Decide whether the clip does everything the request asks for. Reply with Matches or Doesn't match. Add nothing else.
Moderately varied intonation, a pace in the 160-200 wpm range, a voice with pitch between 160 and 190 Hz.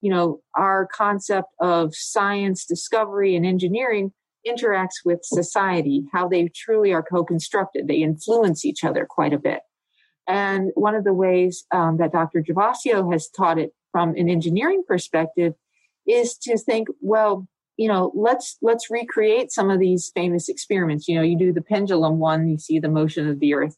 Matches